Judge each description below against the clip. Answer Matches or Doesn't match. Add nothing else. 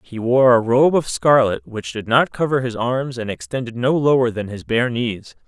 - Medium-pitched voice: Doesn't match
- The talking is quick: Matches